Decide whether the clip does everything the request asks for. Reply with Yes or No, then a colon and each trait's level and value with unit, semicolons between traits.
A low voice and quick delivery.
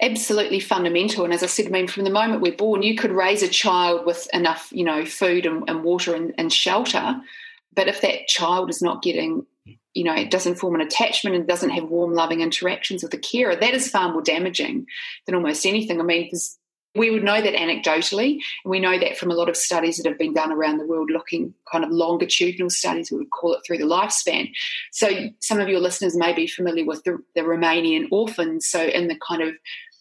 No: medium, 180 Hz; fast, 225 wpm